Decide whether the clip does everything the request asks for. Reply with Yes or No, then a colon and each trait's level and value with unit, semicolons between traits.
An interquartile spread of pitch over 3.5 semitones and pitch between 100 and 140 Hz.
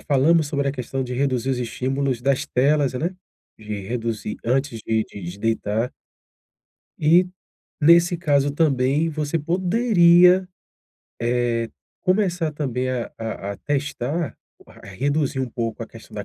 Yes: average, 5.0 semitones; low, 135 Hz